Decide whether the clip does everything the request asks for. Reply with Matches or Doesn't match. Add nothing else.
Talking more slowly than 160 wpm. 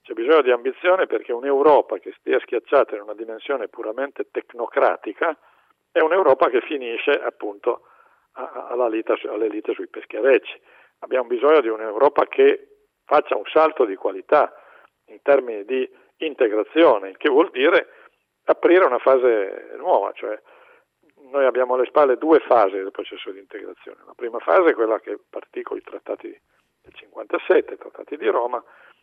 Matches